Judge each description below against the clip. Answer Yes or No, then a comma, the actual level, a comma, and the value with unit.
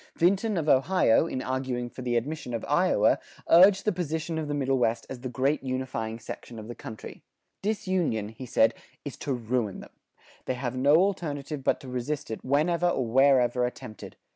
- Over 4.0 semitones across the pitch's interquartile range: Yes, average, 4.6 semitones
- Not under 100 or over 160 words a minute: No, average, 185 wpm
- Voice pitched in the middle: No, low, 130 Hz